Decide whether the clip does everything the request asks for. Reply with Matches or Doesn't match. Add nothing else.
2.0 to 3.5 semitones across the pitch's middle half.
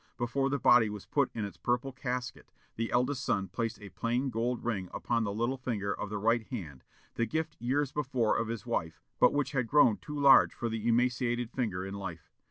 Matches